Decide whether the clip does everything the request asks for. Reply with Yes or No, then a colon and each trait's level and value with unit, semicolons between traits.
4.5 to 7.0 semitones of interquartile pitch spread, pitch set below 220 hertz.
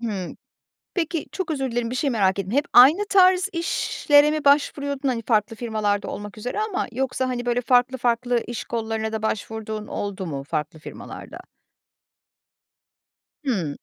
No: average, 4.8 semitones; high, 240 Hz